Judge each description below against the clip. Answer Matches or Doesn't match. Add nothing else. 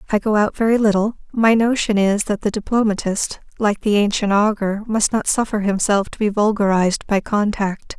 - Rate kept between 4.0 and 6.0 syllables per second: Matches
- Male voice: Doesn't match